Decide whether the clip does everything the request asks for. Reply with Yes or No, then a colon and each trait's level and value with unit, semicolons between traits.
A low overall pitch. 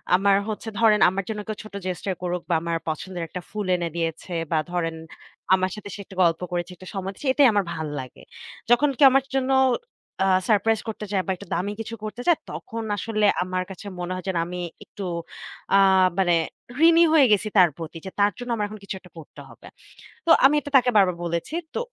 No: high, 195 Hz